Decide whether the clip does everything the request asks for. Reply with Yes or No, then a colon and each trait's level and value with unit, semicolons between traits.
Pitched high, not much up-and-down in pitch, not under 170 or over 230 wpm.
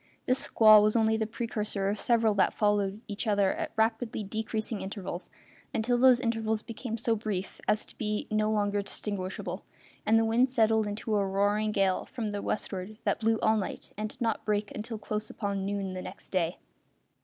Yes: high, 215 Hz; narrow, 1.6 semitones; average, 185 wpm